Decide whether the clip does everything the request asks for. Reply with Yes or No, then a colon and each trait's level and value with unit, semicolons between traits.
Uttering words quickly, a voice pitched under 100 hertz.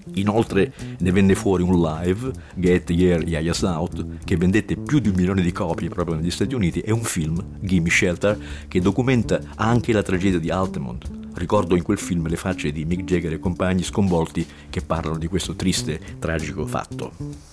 Yes: fast, 180 wpm; very low, 90 Hz